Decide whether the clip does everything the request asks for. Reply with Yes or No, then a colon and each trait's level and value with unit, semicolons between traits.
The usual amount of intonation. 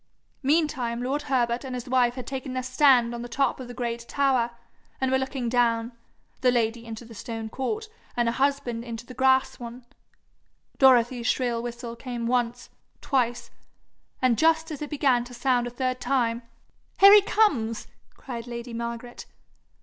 No: narrow, 2.0 semitones